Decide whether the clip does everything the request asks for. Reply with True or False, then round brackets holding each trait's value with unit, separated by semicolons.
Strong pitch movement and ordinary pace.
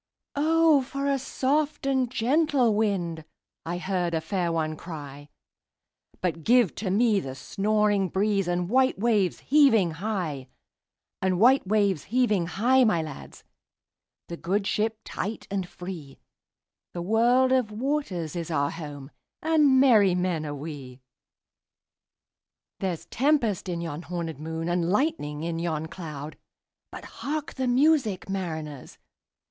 False (7.0 semitones; 115 wpm)